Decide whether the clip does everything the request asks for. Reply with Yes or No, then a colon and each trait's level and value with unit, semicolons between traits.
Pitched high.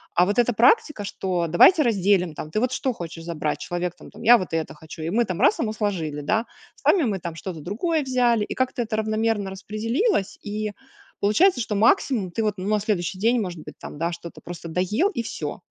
Yes: high, 210 Hz